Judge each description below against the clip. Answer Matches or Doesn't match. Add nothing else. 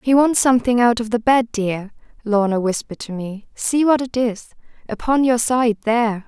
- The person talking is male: Doesn't match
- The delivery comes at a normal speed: Matches